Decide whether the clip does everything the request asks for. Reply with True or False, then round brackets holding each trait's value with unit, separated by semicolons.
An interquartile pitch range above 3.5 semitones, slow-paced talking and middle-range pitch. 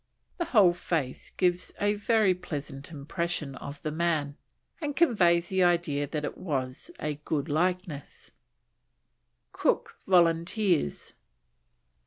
True (3.9 semitones; 115 wpm; 170 Hz)